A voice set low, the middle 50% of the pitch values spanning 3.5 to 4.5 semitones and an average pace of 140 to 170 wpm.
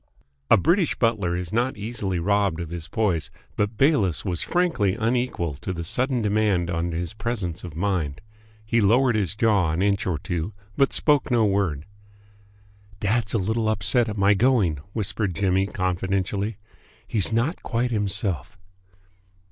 Yes: low, 100 Hz; average, 4.2 semitones; average, 155 wpm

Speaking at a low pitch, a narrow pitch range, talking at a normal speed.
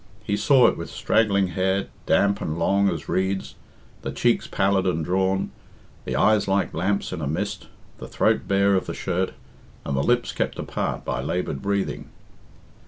Yes: very low, 95 Hz; narrow, 2.3 semitones; average, 170 wpm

